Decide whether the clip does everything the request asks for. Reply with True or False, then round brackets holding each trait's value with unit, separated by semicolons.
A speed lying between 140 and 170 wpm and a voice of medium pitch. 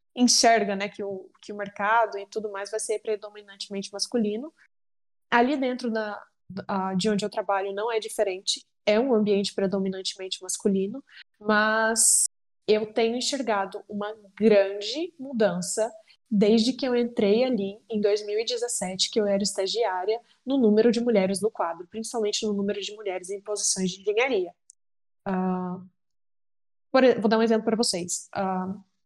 False (145 wpm; 210 Hz)